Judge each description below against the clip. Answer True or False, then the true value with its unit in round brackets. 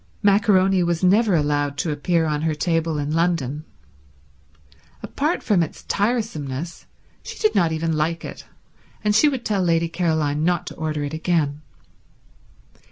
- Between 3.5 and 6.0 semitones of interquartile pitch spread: True (3.8 semitones)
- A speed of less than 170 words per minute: True (150 wpm)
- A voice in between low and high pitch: True (165 Hz)